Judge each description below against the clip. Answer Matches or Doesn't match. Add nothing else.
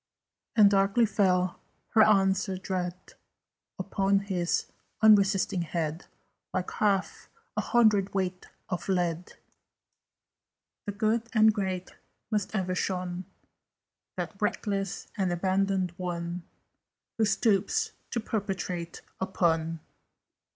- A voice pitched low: Doesn't match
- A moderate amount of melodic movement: Doesn't match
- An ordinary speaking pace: Doesn't match